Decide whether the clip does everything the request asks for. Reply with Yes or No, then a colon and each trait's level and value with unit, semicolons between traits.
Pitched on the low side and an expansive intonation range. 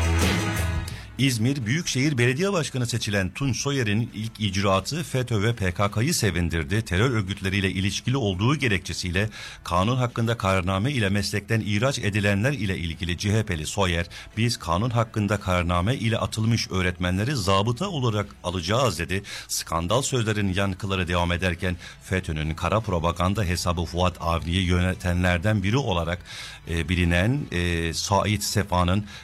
No: low, 100 Hz; average, 4.3 semitones